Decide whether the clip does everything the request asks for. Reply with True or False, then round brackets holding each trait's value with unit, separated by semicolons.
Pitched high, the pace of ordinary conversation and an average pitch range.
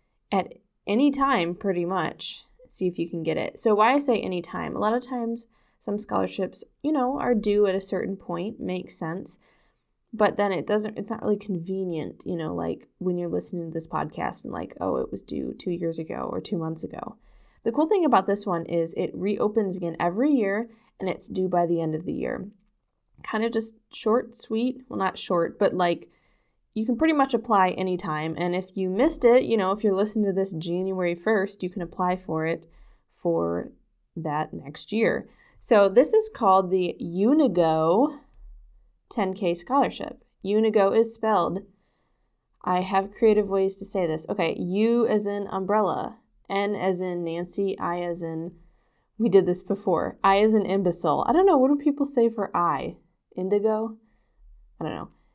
True (195 Hz; 190 wpm; 4.1 semitones)